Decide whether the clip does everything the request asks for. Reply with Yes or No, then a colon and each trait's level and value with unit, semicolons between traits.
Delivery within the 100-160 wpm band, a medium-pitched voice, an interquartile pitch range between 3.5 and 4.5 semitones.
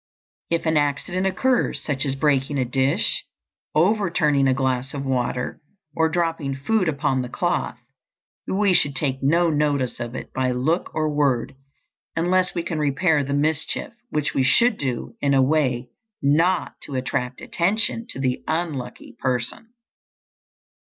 Yes: average, 150 wpm; medium, 145 Hz; average, 4.2 semitones